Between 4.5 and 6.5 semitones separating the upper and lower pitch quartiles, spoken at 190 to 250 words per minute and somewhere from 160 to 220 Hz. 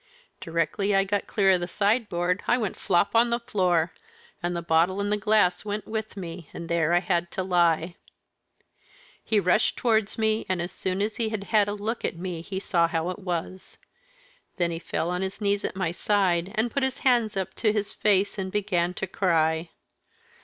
No: average, 3.2 semitones; fast, 205 wpm; high, 190 Hz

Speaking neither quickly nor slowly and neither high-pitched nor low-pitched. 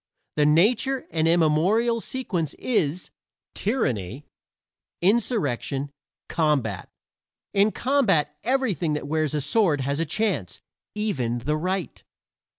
No: slow, 105 wpm; medium, 165 Hz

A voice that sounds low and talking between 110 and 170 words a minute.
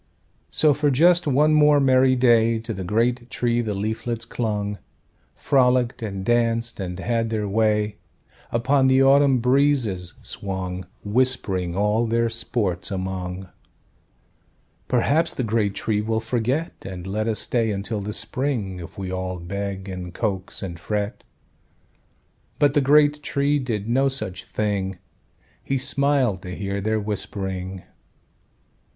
Yes: low, 110 Hz; slow, 135 wpm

